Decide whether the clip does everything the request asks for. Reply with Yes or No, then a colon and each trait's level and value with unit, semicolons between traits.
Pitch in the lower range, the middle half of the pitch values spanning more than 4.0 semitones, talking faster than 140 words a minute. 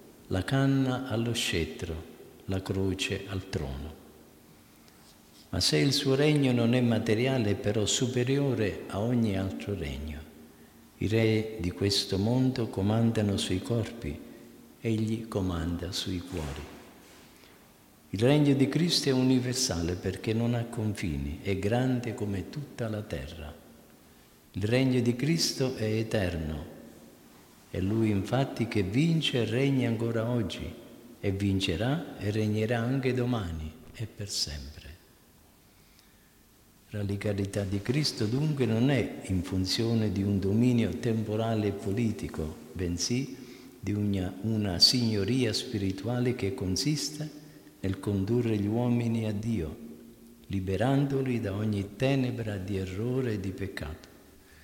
No: low, 110 Hz; average, 4.4 semitones; average, 125 wpm